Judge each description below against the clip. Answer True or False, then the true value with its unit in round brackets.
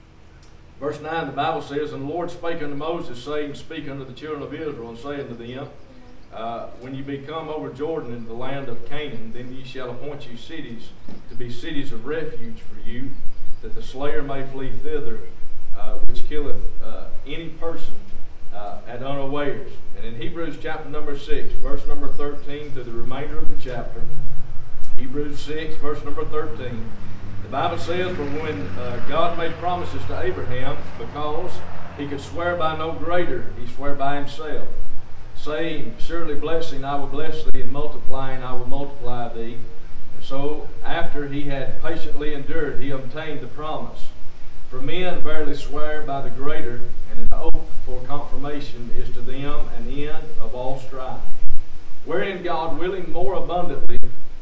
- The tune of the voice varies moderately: True (4.2 semitones)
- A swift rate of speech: False (170 wpm)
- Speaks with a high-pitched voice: False (140 Hz)